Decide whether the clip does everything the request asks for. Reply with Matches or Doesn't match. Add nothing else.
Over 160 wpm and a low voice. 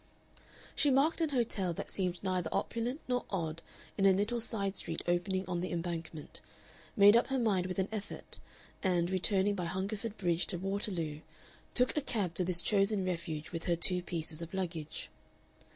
Doesn't match